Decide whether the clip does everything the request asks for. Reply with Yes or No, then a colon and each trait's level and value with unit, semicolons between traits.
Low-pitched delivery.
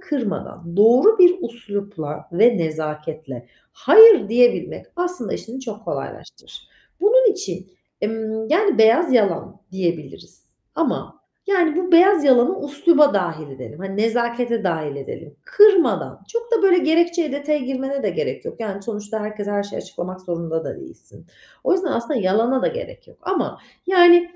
No: high, 235 Hz